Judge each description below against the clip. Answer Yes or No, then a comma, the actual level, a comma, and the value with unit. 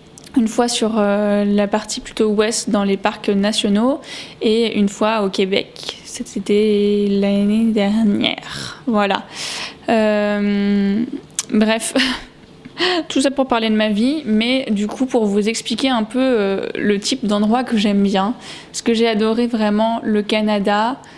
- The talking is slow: Yes, slow, 140 wpm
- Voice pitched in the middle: No, high, 220 Hz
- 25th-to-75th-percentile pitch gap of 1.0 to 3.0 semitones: Yes, narrow, 2.6 semitones